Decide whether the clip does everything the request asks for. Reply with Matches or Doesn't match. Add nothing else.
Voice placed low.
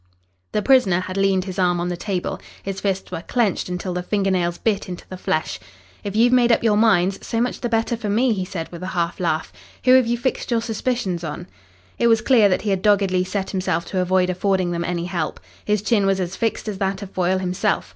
Doesn't match